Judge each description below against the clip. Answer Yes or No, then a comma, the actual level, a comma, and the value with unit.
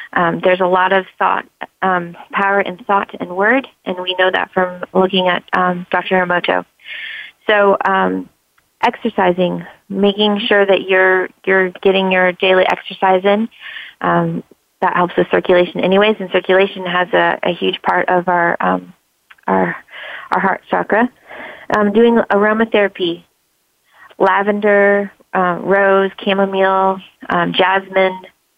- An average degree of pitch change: No, narrow, 1.8 semitones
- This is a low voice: No, high, 190 Hz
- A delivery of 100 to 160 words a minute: Yes, slow, 135 wpm